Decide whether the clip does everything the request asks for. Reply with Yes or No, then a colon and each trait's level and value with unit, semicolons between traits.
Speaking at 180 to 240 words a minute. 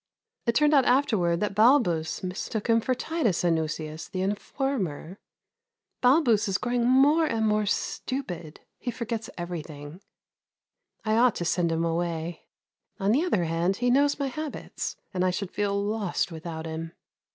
No: average, 150 wpm